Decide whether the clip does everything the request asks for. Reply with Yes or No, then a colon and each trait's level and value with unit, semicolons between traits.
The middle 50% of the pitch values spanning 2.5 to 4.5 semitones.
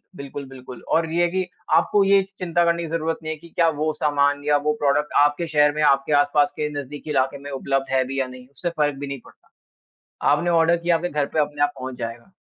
Yes: average, 3.1 semitones